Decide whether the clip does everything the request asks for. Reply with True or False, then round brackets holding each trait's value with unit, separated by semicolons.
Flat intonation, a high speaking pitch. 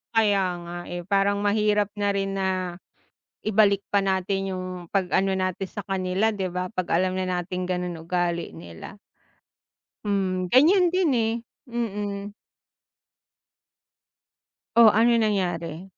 True (2.3 semitones; 195 Hz)